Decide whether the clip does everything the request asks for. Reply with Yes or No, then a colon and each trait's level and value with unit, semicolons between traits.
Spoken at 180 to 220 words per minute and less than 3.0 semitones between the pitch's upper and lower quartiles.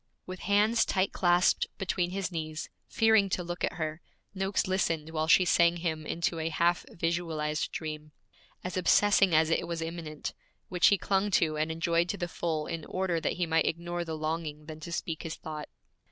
Yes: average, 190 wpm; narrow, 2.5 semitones